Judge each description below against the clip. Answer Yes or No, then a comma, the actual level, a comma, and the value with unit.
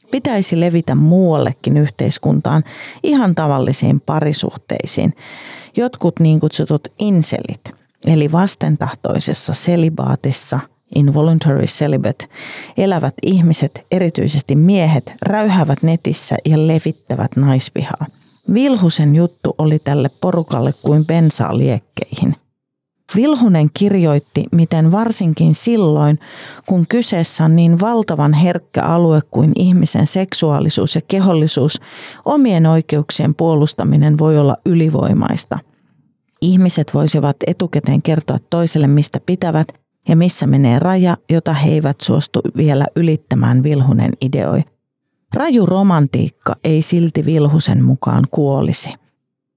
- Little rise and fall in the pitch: No, average, 3.1 semitones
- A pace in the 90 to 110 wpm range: Yes, average, 100 wpm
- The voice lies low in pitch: No, medium, 155 Hz